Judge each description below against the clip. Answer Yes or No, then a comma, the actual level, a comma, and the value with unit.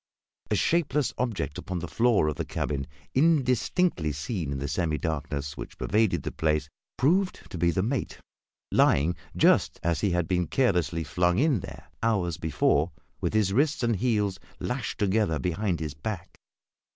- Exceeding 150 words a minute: Yes, average, 165 wpm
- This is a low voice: Yes, very low, 90 Hz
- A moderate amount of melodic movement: No, wide, 6.8 semitones